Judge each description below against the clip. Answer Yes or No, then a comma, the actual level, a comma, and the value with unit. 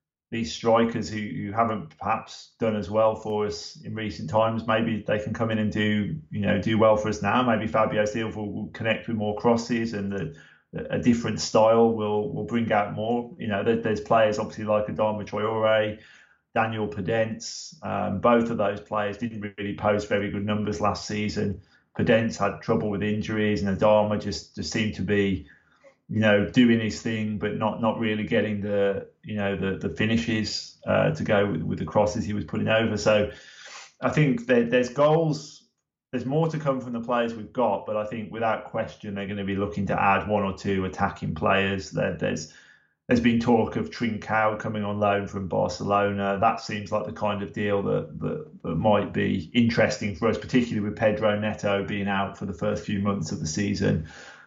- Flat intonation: Yes, narrow, 1.6 semitones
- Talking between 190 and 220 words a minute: Yes, average, 200 wpm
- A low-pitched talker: Yes, low, 105 Hz